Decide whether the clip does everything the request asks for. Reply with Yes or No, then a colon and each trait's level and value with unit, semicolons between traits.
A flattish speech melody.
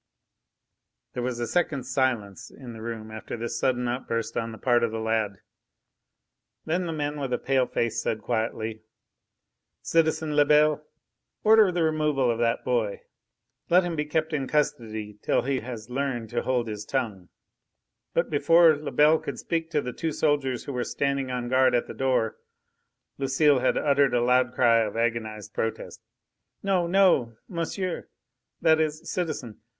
No: average, 4.7 semitones